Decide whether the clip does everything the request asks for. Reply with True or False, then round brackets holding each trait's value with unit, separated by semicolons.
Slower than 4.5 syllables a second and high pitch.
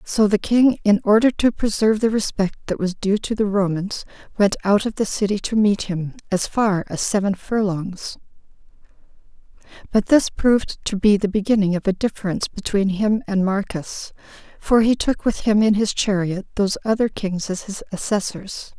False (5.0 syllables/s; 205 Hz)